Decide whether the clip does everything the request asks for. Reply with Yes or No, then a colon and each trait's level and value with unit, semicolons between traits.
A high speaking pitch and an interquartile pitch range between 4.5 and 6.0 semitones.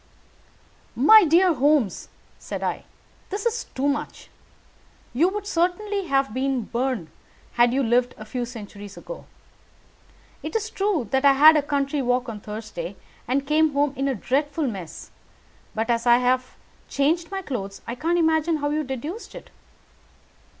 Yes: very high, 275 Hz; average, 5.2 semitones